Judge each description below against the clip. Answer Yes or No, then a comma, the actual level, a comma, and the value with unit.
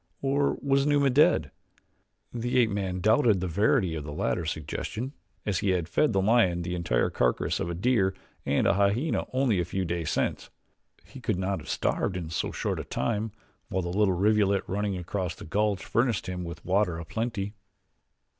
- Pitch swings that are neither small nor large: Yes, average, 4.2 semitones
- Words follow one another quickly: No, average, 190 wpm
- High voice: No, very low, 95 Hz